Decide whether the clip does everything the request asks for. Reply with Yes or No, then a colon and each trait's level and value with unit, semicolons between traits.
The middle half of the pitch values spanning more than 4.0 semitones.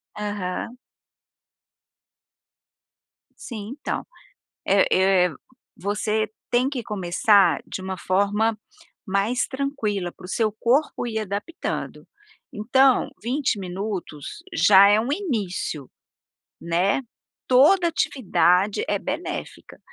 Yes: average, 4.5 semitones